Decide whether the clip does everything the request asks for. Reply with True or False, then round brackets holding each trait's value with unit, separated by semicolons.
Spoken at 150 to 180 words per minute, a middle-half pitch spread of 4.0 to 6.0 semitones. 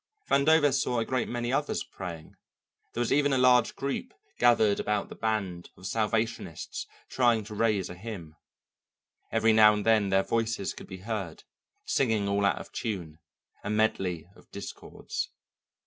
False (160 wpm; 3.5 semitones)